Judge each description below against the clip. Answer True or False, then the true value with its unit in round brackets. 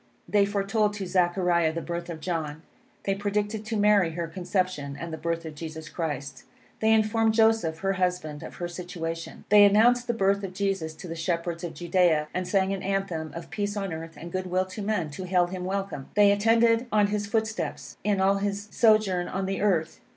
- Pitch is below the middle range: False (185 Hz)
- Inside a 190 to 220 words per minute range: True (200 wpm)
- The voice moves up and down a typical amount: True (3.4 semitones)